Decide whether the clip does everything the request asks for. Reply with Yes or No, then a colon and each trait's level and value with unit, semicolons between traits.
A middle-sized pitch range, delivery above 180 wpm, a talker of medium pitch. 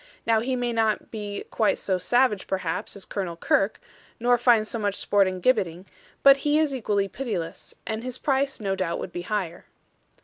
No: average, 4.4 semitones; average, 190 wpm; high, 215 Hz